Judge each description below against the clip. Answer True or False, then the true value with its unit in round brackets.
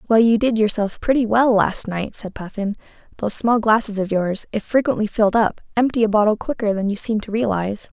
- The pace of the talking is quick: True (210 wpm)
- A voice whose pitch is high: True (215 Hz)